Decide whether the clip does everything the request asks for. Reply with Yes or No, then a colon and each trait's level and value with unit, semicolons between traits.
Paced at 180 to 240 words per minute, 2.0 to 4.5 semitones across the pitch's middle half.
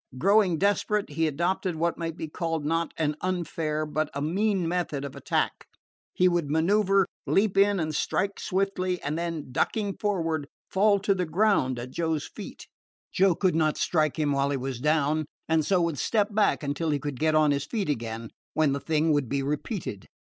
Yes: average, 190 wpm; average, 4.2 semitones